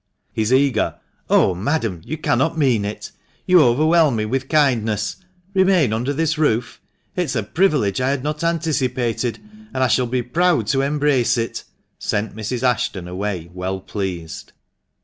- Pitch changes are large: Yes, wide, 5.8 semitones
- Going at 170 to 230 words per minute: No, average, 155 wpm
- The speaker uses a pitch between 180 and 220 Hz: No, low, 125 Hz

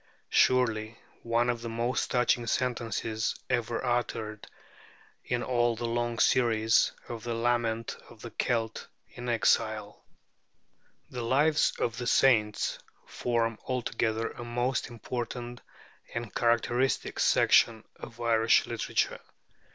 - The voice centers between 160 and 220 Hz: No, low, 120 Hz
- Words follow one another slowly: Yes, slow, 120 wpm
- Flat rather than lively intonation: Yes, narrow, 1.3 semitones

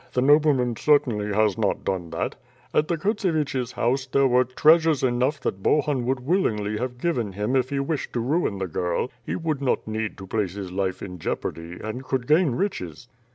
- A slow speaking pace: No, average, 195 wpm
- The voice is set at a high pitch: No, low, 125 Hz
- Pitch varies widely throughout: Yes, wide, 5.9 semitones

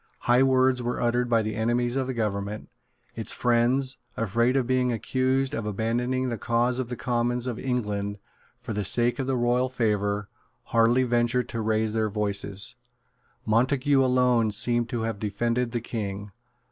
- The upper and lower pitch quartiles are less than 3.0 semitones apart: Yes, narrow, 2.4 semitones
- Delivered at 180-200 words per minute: No, average, 160 wpm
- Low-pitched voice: Yes, low, 120 Hz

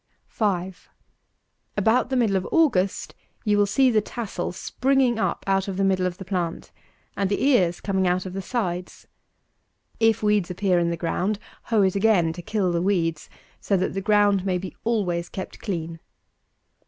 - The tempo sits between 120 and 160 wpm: No, average, 180 wpm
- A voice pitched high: Yes, high, 195 Hz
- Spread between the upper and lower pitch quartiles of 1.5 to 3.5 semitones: Yes, average, 2.9 semitones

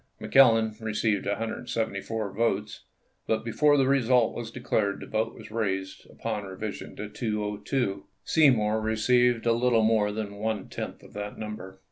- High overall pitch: No, low, 110 Hz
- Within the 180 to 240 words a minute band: No, average, 145 wpm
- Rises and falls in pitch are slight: Yes, narrow, 2.0 semitones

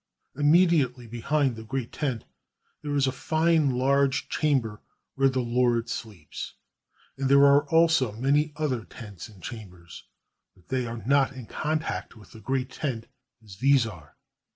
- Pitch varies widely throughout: No, average, 3.9 semitones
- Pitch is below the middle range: Yes, low, 130 Hz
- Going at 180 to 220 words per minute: No, average, 155 wpm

